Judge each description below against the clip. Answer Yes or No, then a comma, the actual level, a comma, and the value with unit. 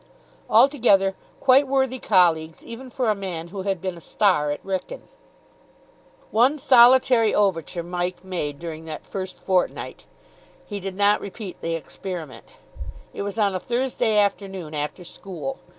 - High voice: Yes, high, 195 Hz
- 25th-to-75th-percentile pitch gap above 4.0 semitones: Yes, average, 4.9 semitones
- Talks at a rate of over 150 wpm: No, average, 145 wpm